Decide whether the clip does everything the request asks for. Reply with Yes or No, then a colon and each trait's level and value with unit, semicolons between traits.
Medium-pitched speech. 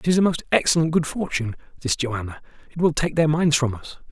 Yes: medium, 145 Hz